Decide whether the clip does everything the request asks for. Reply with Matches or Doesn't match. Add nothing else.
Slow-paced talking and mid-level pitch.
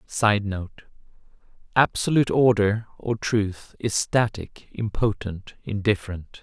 Doesn't match